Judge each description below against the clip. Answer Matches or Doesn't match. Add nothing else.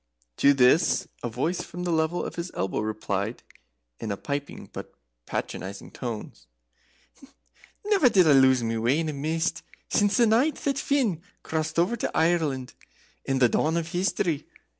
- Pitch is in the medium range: Matches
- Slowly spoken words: Doesn't match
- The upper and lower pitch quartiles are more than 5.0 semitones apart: Matches